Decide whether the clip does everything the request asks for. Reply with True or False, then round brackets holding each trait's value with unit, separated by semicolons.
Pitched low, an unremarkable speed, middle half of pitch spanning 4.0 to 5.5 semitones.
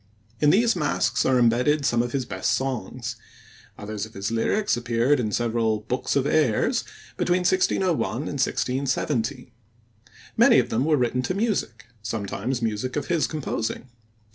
True (125 Hz; 150 wpm; 4.5 semitones)